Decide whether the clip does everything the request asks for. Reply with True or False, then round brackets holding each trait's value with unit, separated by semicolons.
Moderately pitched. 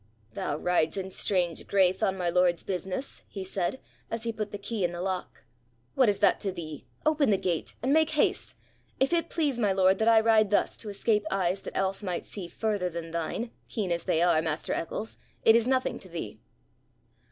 False (195 Hz)